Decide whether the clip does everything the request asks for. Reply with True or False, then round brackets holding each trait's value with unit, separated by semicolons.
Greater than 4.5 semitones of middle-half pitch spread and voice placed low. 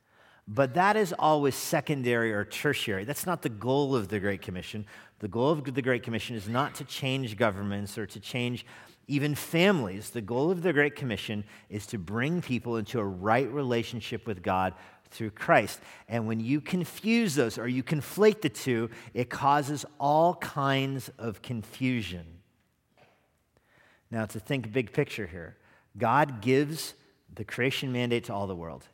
True (4.9 semitones; 125 Hz)